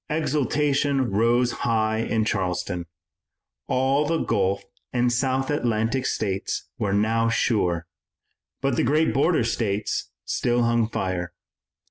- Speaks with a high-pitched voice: No, low, 115 Hz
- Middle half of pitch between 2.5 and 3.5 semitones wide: No, average, 4.2 semitones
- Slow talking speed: Yes, slow, 115 wpm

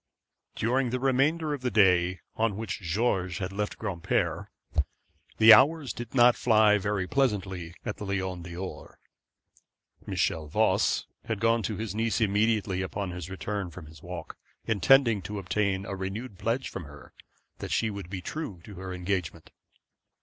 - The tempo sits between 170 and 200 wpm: No, average, 155 wpm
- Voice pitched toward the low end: Yes, low, 100 Hz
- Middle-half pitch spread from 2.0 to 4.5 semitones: Yes, average, 3.9 semitones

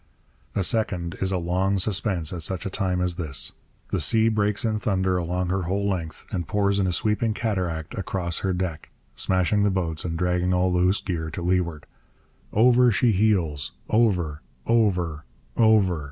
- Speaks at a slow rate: No, average, 170 wpm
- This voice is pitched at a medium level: No, very low, 95 Hz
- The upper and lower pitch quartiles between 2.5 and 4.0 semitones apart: Yes, average, 3.0 semitones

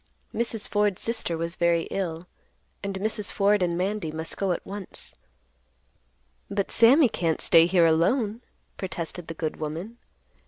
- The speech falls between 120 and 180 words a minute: Yes, average, 145 wpm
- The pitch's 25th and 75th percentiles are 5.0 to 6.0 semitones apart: No, average, 3.8 semitones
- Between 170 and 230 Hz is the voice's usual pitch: Yes, high, 190 Hz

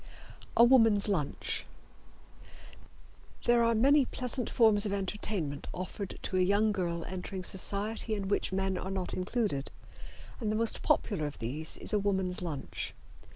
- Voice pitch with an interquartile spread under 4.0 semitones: Yes, average, 3.2 semitones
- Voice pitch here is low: No, high, 200 Hz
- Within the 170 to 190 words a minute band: No, average, 150 wpm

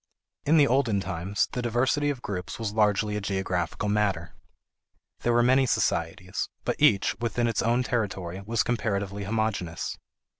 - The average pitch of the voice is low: Yes, low, 105 Hz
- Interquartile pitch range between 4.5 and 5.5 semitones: No, average, 3.5 semitones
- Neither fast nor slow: Yes, average, 150 wpm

